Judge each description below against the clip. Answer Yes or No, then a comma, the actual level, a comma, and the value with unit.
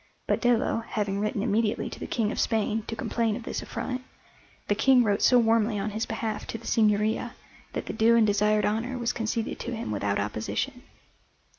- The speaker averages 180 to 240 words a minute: Yes, average, 195 wpm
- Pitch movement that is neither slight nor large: No, narrow, 1.8 semitones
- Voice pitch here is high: Yes, high, 220 Hz